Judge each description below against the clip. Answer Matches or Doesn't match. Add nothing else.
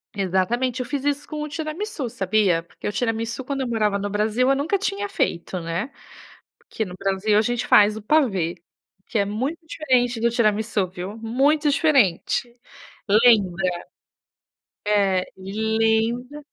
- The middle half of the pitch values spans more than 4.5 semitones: Matches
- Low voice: Doesn't match